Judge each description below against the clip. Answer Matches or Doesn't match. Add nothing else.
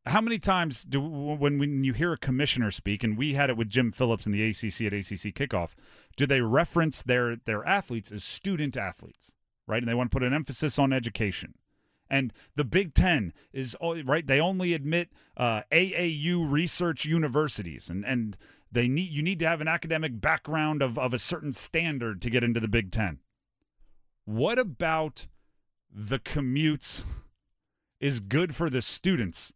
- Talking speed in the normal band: Matches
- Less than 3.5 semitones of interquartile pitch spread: Doesn't match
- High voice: Doesn't match